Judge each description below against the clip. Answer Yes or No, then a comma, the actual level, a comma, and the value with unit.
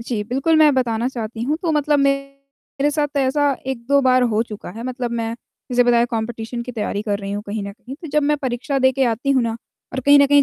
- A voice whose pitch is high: Yes, very high, 255 Hz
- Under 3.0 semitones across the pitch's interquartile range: No, average, 3.3 semitones